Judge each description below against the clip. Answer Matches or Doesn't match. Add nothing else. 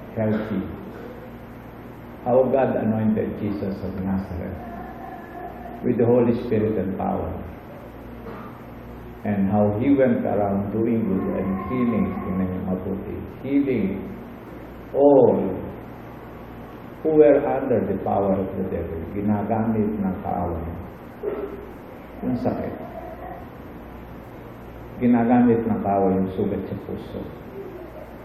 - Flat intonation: Doesn't match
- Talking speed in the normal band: Doesn't match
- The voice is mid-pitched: Doesn't match